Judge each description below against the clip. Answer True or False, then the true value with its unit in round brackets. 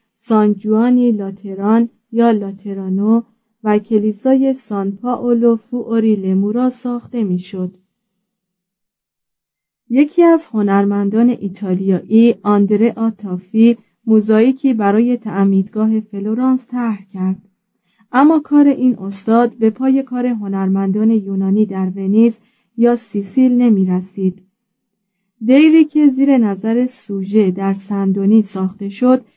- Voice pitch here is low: False (220 Hz)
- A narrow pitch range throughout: False (3.4 semitones)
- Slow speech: True (100 wpm)